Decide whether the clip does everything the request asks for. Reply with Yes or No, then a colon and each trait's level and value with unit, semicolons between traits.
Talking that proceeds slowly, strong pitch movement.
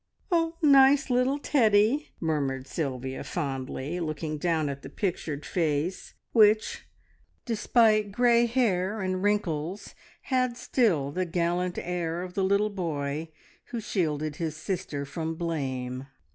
Yes: slow, 120 wpm; wide, 6.0 semitones